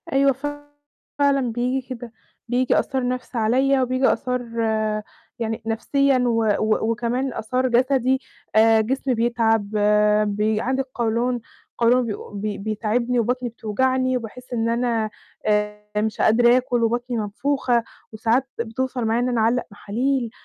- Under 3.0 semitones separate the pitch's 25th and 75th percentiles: Yes, narrow, 2.4 semitones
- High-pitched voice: Yes, high, 240 Hz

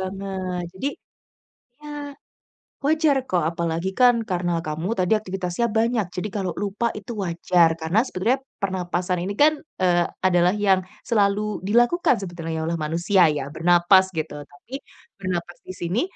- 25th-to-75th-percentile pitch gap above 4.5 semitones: No, average, 3.3 semitones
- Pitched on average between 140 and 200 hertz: Yes, medium, 185 Hz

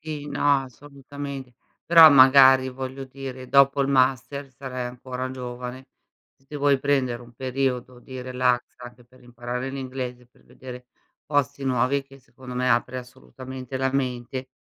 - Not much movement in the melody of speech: Yes, narrow, 1.4 semitones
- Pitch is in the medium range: No, low, 130 Hz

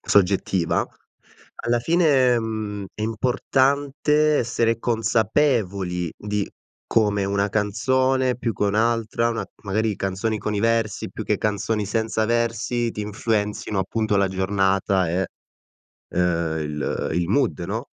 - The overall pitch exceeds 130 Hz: No, low, 110 Hz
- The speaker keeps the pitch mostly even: No, average, 3.1 semitones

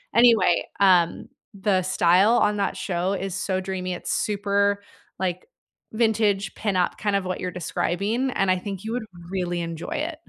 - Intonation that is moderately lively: No, narrow, 2.3 semitones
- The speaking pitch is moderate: No, high, 195 Hz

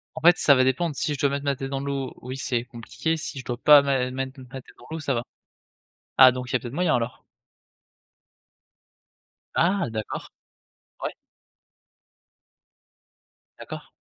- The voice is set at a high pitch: No, low, 135 Hz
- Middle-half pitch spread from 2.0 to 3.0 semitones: Yes, narrow, 2.4 semitones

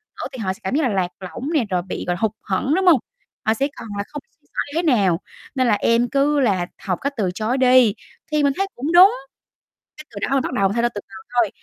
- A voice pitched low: No, high, 240 Hz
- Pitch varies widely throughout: Yes, wide, 5.8 semitones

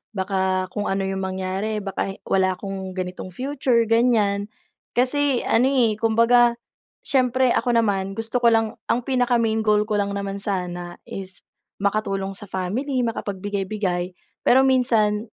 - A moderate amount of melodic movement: Yes, average, 3.8 semitones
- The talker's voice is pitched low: No, high, 210 Hz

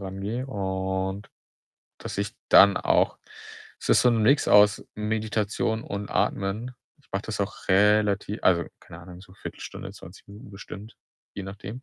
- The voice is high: No, low, 100 Hz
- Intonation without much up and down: Yes, narrow, 1.9 semitones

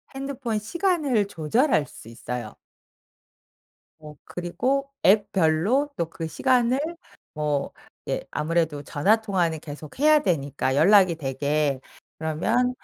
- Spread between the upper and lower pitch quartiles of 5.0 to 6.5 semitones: No, wide, 8.3 semitones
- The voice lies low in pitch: No, medium, 175 Hz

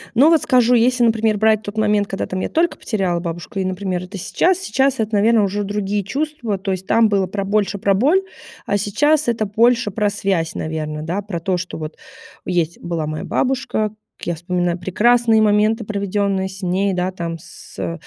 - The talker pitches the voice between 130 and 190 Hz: No, high, 205 Hz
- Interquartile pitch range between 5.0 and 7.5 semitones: No, average, 3.6 semitones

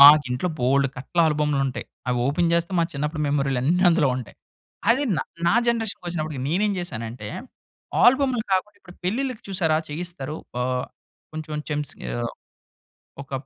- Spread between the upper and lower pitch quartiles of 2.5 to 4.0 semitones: No, average, 4.8 semitones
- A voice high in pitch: No, medium, 150 Hz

